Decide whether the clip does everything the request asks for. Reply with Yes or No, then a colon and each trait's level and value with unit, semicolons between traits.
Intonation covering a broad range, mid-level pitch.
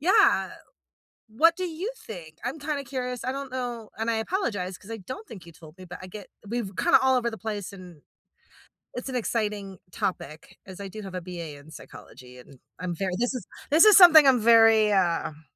No: wide, 6.0 semitones; high, 220 Hz